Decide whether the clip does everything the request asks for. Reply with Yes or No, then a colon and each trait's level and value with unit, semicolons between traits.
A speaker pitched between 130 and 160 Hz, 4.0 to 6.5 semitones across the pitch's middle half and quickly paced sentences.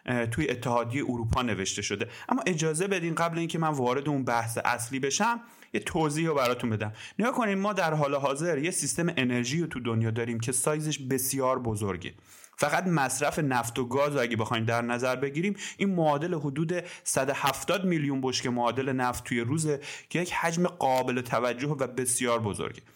Yes: low, 135 Hz; average, 5.2 semitones; fast, 180 wpm